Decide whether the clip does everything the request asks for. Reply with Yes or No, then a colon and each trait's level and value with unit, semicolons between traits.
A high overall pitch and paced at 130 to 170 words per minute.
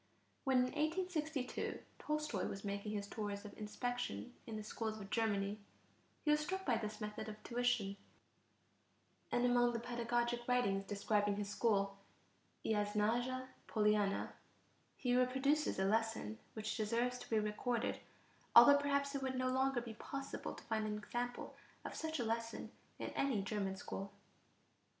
Yes: high, 230 Hz; average, 150 wpm